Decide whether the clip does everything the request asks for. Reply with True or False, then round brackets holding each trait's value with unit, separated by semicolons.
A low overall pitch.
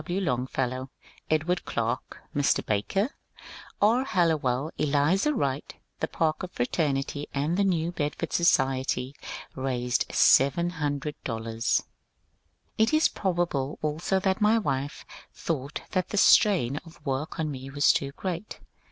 False (150 Hz)